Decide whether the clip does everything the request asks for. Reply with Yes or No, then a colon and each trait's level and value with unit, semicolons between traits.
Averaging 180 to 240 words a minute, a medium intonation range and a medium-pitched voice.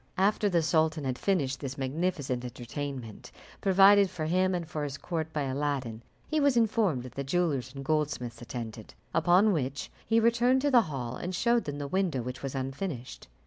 No: average, 185 wpm; wide, 6.1 semitones; medium, 150 Hz